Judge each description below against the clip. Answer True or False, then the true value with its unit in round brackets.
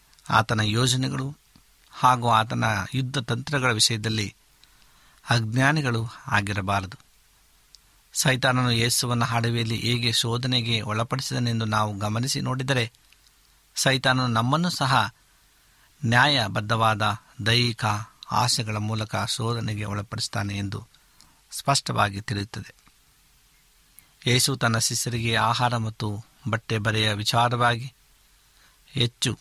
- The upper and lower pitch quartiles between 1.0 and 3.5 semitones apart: True (2.8 semitones)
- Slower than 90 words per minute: True (80 wpm)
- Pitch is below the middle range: True (115 Hz)